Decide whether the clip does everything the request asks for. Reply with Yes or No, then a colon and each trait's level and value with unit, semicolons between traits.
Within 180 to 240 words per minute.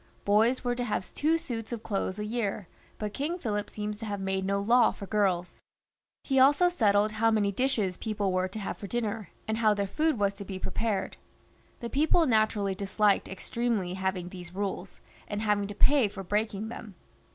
Yes: average, 195 wpm